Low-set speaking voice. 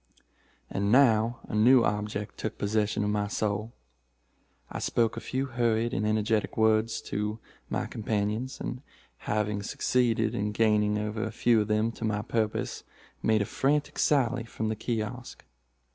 Yes: low, 110 Hz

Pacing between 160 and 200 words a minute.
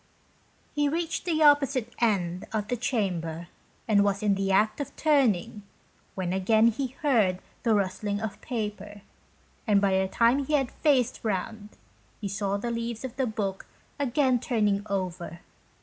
No: average, 150 wpm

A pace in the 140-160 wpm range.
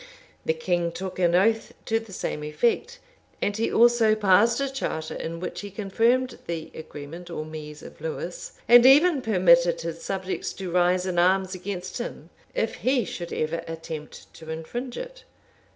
No: average, 170 wpm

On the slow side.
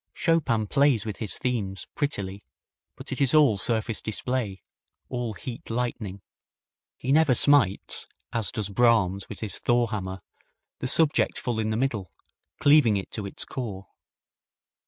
No: average, 145 wpm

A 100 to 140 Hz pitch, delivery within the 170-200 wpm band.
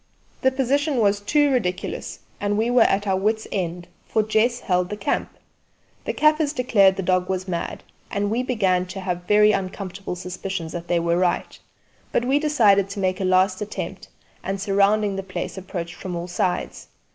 No: high, 195 Hz; average, 180 wpm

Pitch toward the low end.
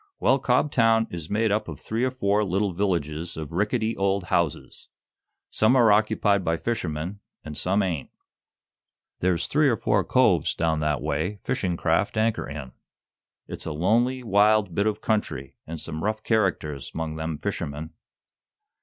Yes: low, 100 Hz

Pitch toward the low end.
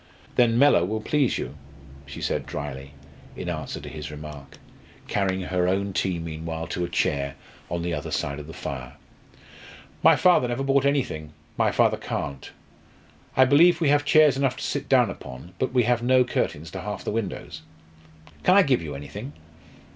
Yes: very low, 95 Hz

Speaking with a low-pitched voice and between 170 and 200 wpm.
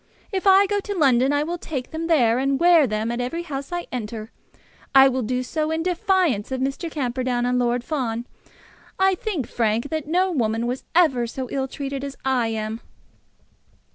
No: very high, 270 Hz; average, 190 wpm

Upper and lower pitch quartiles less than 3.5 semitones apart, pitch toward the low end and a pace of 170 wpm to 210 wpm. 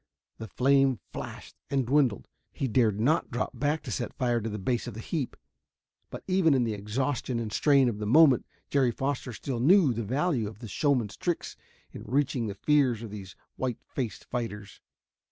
No: average, 4.0 semitones; low, 125 Hz; average, 190 wpm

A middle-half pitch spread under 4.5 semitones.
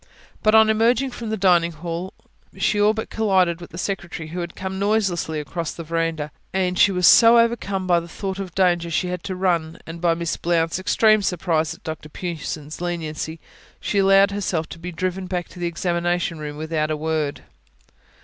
Yes: average, 2.7 semitones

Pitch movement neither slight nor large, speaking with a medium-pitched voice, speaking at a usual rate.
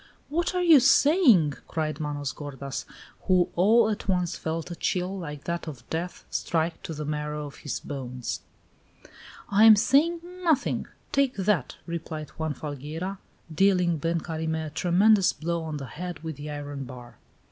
Yes: average, 4.7 semitones; medium, 165 Hz; average, 160 wpm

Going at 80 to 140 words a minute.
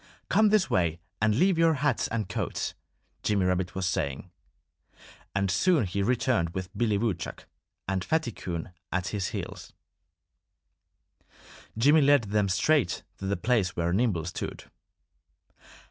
Yes: slow, 135 wpm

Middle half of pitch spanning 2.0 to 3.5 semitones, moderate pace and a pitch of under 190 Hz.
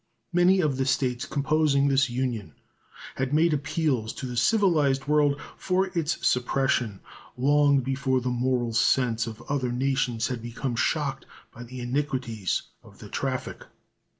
Yes: average, 3.2 semitones; average, 145 wpm; low, 135 Hz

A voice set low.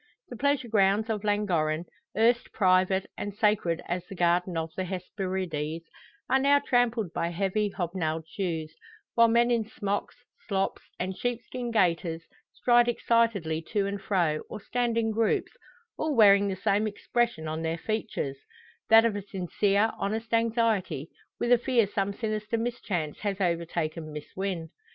No: high, 200 Hz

